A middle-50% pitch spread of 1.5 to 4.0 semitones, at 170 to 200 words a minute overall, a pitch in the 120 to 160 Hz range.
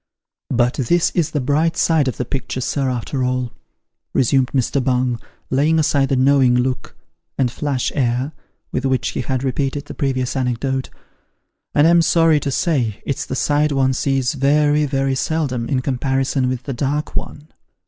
Yes: narrow, 2.4 semitones; average, 175 wpm; low, 135 Hz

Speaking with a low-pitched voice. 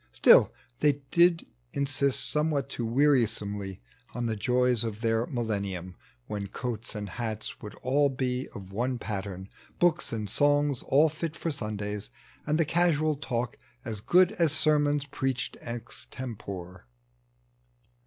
Yes: low, 125 Hz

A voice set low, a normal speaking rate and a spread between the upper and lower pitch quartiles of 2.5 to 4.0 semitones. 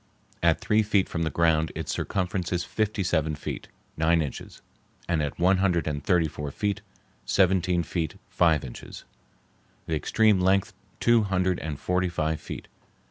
Yes: very low, 85 Hz; average, 155 wpm; average, 3.1 semitones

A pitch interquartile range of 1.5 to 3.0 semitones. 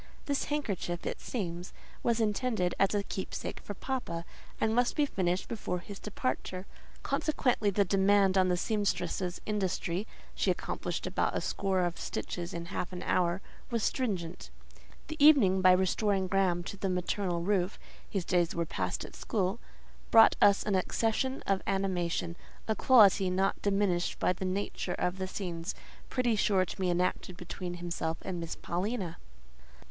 Yes: average, 2.7 semitones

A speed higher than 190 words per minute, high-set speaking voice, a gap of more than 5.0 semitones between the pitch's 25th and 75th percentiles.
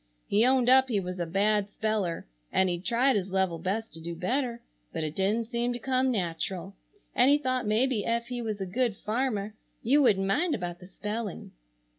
No: average, 200 wpm; high, 215 Hz; average, 4.5 semitones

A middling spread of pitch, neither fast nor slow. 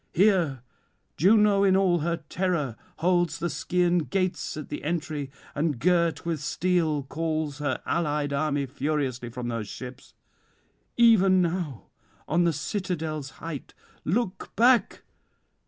No: average, 4.0 semitones; slow, 125 wpm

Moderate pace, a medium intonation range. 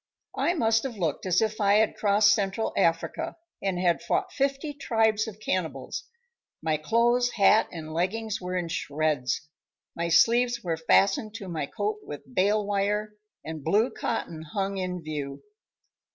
Yes: average, 155 wpm; average, 5.0 semitones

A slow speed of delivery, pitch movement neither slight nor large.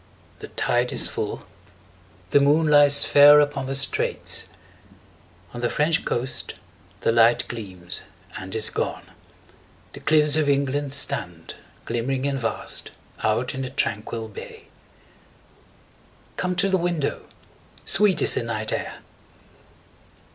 Yes: slow, 130 wpm; average, 4.1 semitones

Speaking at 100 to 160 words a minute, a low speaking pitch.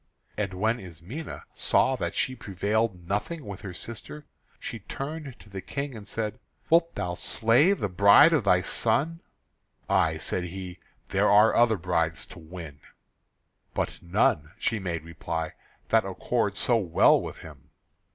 Yes: average, 150 wpm; low, 100 Hz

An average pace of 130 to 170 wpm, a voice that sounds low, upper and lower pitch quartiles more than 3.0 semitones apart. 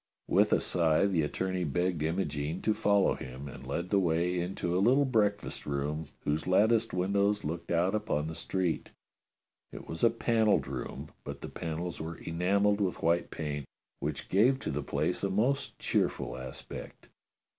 Yes: average, 165 wpm; very low, 90 Hz; average, 4.2 semitones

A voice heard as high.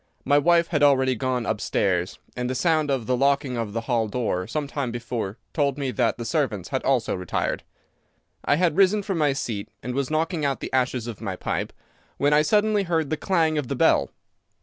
No: low, 135 Hz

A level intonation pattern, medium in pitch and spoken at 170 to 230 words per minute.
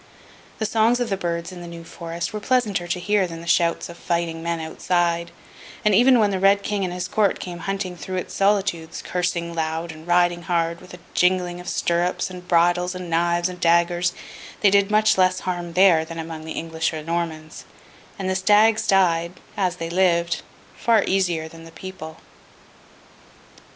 Yes: narrow, 2.1 semitones; medium, 175 Hz; average, 185 wpm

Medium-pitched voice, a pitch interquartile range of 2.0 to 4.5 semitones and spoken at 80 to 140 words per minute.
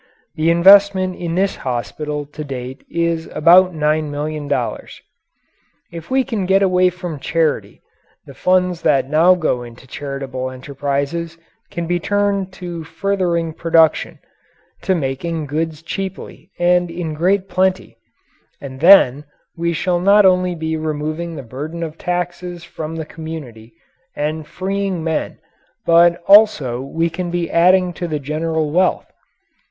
Yes: medium, 165 Hz; average, 3.2 semitones; slow, 135 wpm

